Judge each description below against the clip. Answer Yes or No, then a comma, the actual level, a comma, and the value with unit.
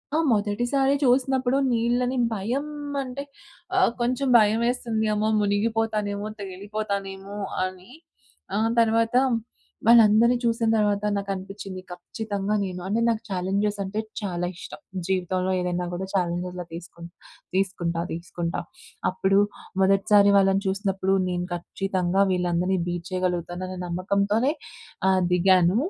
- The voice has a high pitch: Yes, high, 200 Hz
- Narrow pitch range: No, average, 3.3 semitones